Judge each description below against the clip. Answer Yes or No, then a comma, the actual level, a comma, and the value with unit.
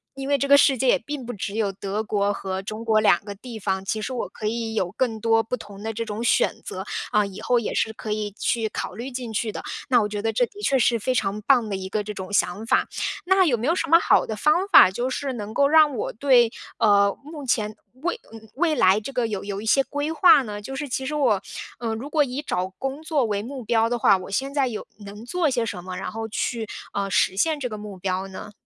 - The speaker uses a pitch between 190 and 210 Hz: No, high, 225 Hz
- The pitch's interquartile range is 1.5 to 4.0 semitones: No, average, 4.5 semitones